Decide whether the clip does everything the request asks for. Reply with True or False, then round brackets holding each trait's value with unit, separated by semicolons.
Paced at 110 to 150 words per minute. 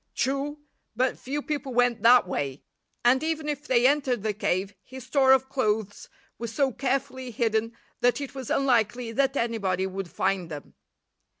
False (165 wpm)